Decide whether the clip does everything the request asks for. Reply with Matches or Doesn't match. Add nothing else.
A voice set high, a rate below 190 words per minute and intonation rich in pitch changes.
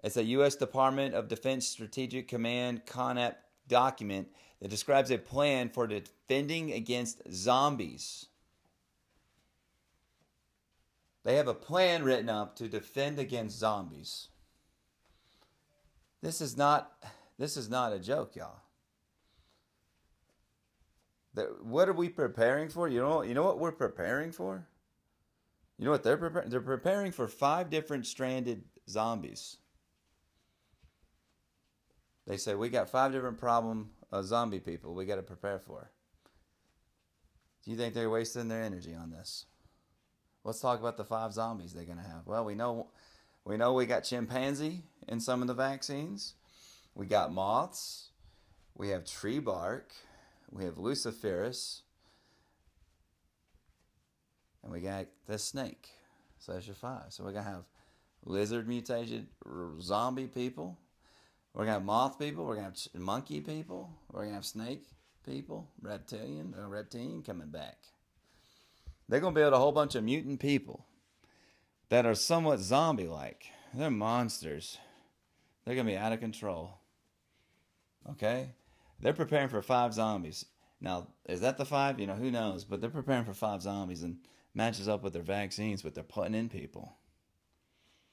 Doesn't match